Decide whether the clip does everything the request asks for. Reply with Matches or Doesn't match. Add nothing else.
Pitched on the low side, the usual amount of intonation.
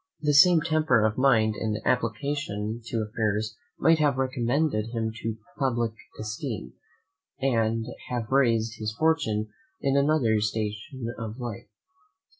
Matches